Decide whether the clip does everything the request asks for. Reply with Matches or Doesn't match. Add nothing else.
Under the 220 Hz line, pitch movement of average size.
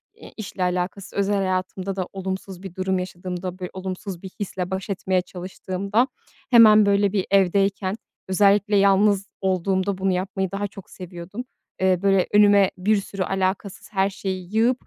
Doesn't match